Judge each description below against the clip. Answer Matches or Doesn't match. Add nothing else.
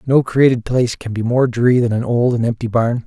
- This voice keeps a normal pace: Doesn't match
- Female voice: Doesn't match